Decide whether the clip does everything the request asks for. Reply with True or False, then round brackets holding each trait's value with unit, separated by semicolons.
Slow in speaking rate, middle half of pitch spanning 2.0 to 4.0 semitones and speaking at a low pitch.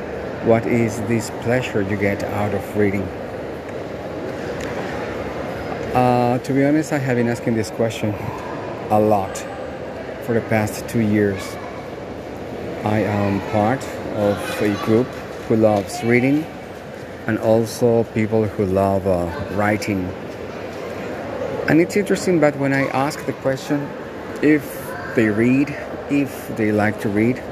True (130 wpm; 3.1 semitones; 110 Hz)